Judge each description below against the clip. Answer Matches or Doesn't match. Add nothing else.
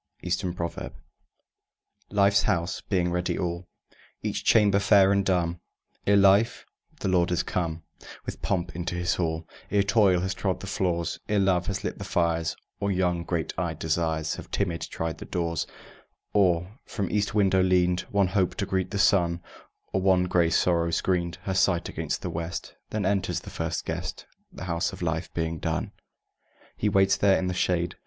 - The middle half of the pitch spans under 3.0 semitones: Matches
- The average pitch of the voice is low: Matches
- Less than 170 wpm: Doesn't match